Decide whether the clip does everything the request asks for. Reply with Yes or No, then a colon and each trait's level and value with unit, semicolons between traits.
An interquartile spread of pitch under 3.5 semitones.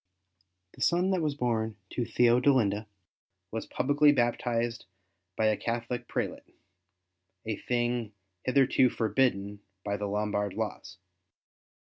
Yes: average, 3.0 semitones